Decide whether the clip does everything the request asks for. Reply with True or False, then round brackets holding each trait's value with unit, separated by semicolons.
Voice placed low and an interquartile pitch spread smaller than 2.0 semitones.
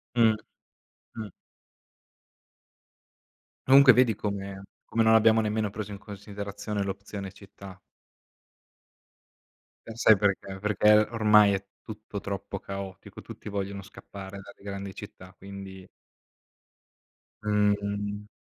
True (100 Hz; 1.5 semitones)